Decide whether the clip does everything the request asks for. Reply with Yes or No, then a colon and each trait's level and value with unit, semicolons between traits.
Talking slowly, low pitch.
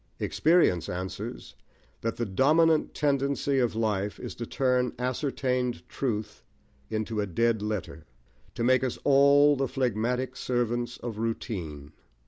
Yes: slow, 125 wpm; low, 120 Hz